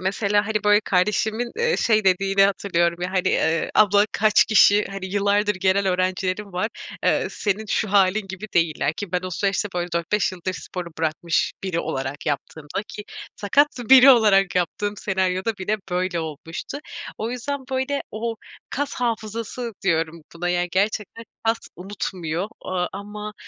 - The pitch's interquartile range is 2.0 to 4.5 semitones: Yes, average, 2.9 semitones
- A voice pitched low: No, high, 195 Hz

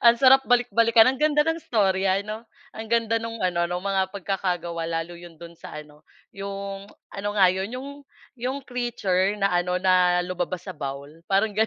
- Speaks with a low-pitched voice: No, high, 195 Hz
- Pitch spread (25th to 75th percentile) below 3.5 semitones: No, average, 4.4 semitones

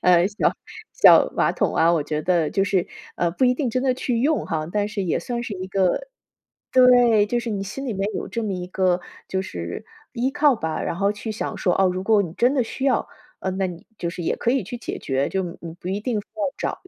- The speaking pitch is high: Yes, high, 200 Hz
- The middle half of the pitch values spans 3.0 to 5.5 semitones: Yes, average, 5.2 semitones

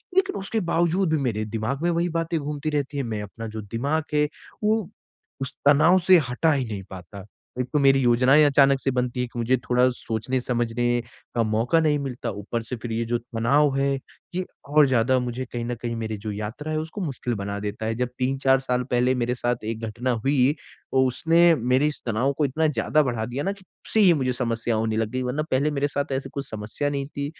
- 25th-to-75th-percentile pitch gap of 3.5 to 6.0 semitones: Yes, average, 4.0 semitones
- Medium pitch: No, low, 130 Hz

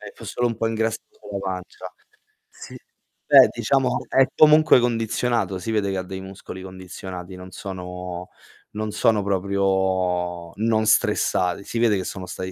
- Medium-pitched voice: No, very low, 95 Hz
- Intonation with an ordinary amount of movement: Yes, average, 3.4 semitones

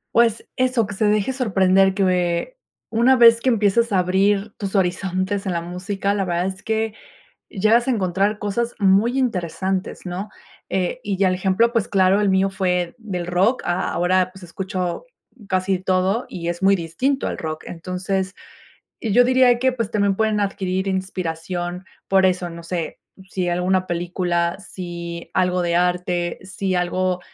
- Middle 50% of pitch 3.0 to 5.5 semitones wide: No, narrow, 2.5 semitones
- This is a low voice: No, high, 190 Hz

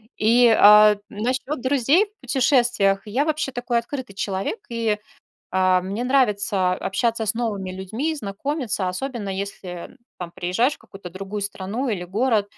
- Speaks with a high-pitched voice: Yes, high, 215 Hz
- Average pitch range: Yes, average, 4.7 semitones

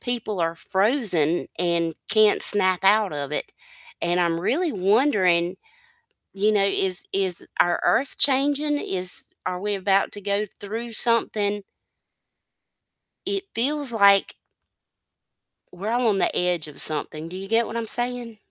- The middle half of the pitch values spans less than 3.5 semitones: No, average, 4.5 semitones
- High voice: Yes, high, 200 Hz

